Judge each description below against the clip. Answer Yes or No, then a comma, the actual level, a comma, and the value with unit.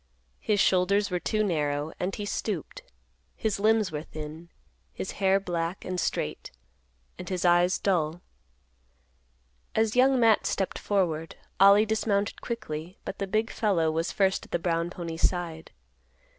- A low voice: No, medium, 185 Hz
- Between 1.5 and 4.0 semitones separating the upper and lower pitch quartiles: Yes, average, 3.7 semitones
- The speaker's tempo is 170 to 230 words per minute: No, average, 145 wpm